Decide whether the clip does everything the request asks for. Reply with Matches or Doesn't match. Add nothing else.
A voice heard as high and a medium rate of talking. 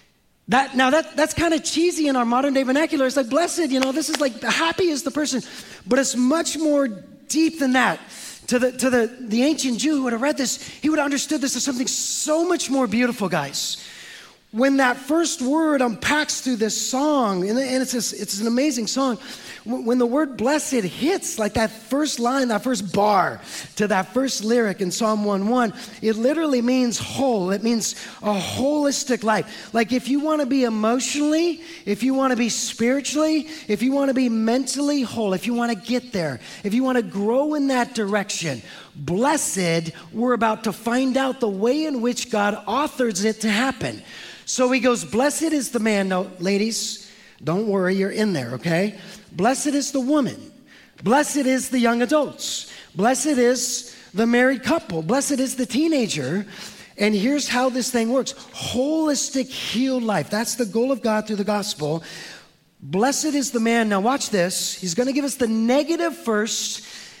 Matches